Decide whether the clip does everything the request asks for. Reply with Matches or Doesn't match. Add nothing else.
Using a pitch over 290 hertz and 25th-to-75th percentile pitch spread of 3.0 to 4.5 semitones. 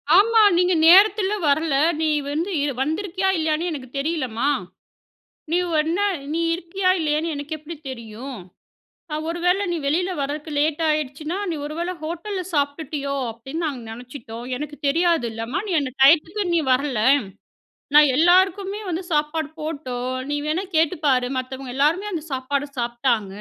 Matches